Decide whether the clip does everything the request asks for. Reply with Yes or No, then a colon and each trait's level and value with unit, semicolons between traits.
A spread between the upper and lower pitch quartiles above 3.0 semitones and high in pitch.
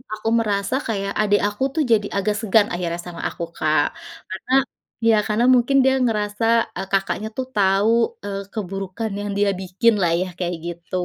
No: narrow, 2.6 semitones; high, 205 Hz